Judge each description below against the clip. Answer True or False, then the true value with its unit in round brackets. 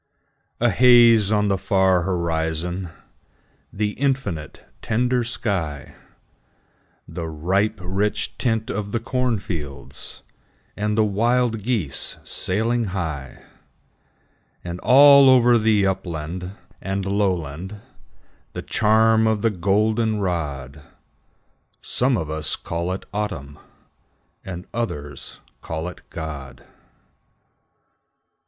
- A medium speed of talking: False (95 wpm)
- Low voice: True (100 Hz)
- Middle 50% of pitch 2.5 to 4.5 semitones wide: False (4.9 semitones)